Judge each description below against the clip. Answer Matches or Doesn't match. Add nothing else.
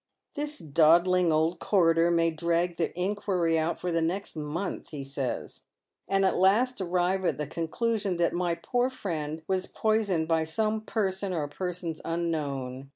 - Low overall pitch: Doesn't match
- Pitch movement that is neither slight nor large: Matches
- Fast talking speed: Doesn't match